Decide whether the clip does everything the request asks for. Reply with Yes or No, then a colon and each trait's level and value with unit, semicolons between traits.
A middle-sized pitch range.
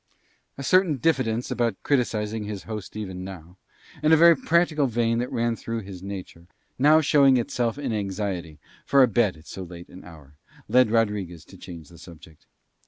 No: wide, 5.7 semitones